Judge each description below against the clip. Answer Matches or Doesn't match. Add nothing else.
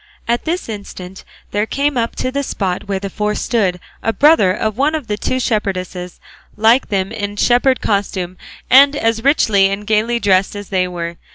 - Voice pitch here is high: Matches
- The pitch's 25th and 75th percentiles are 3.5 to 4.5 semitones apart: Matches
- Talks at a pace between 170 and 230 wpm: Matches